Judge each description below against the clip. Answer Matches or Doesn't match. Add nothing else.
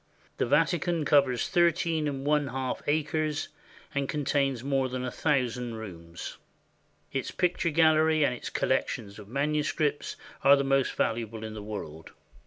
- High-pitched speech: Doesn't match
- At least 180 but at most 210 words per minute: Doesn't match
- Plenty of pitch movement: Doesn't match